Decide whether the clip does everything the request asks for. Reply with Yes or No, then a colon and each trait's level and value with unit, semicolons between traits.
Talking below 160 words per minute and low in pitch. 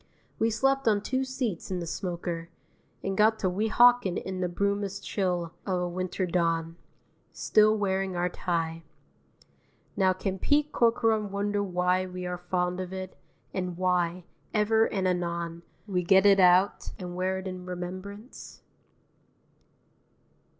No: average, 145 wpm; medium, 185 Hz